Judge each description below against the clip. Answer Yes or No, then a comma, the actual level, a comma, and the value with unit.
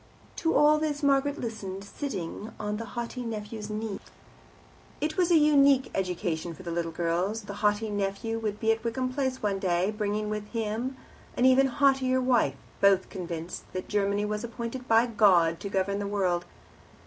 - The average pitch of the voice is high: Yes, high, 215 Hz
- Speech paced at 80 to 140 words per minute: No, average, 170 wpm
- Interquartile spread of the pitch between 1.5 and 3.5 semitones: No, average, 4.6 semitones